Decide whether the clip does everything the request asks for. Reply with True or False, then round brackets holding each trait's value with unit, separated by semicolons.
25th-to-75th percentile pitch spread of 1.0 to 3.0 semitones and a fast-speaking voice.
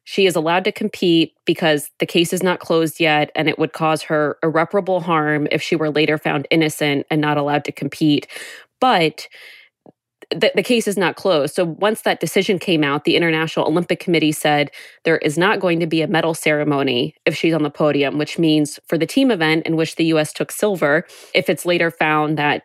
True (2.5 semitones; 210 wpm)